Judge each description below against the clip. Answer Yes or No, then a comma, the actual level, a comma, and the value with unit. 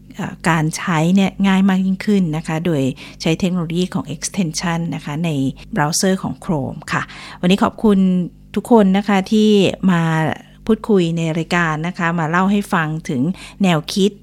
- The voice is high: No, medium, 180 Hz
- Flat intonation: No, average, 3.2 semitones